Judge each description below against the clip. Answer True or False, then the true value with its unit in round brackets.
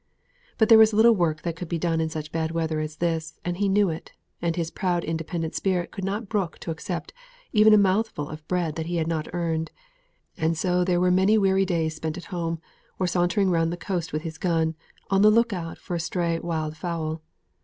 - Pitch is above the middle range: False (170 Hz)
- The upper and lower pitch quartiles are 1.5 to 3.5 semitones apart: True (2.8 semitones)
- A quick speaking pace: True (225 wpm)